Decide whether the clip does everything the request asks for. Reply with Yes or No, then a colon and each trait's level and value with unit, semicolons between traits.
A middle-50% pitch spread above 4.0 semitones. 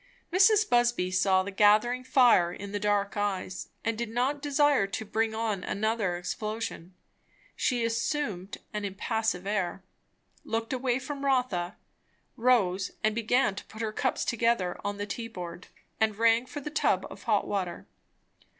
No: average, 3.6 semitones